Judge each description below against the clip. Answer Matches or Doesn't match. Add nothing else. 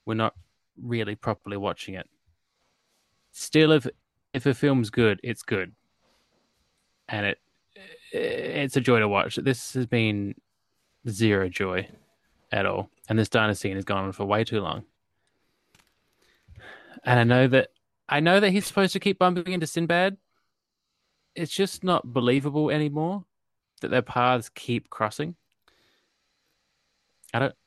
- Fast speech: Doesn't match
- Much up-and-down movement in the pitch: Matches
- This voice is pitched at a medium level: Doesn't match